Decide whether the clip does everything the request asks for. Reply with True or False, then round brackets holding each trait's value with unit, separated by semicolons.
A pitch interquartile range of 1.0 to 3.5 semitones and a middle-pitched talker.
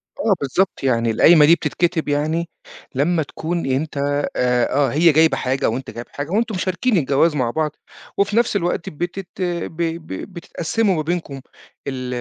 False (4.2 semitones; 160 Hz)